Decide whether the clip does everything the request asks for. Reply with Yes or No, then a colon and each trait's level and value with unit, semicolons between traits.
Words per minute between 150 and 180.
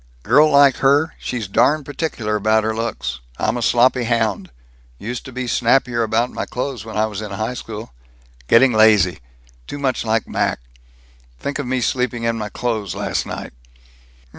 Yes: average, 170 wpm